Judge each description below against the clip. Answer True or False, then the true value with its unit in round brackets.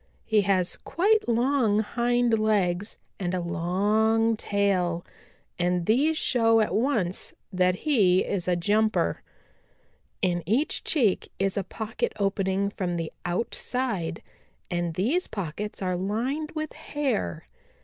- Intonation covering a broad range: False (4.5 semitones)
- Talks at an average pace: False (125 wpm)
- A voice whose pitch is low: False (205 Hz)